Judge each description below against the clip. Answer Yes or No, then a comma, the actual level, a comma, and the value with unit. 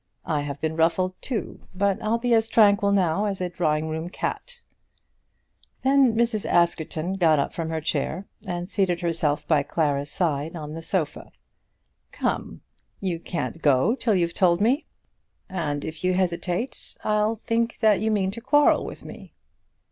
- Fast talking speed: No, average, 165 wpm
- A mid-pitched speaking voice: Yes, medium, 180 Hz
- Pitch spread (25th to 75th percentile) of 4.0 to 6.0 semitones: Yes, average, 4.9 semitones